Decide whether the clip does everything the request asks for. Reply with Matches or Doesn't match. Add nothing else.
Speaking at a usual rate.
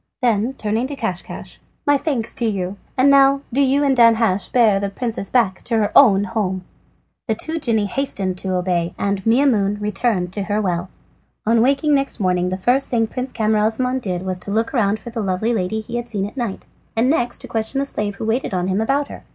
Doesn't match